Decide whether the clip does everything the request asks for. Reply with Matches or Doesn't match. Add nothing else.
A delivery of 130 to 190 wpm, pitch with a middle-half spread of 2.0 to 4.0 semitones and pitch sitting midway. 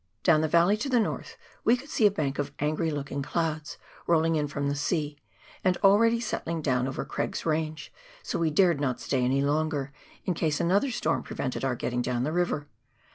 Doesn't match